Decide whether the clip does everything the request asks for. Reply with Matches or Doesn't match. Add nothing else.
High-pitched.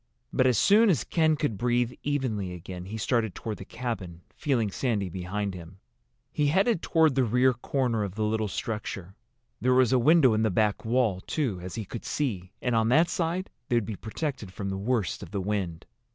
Doesn't match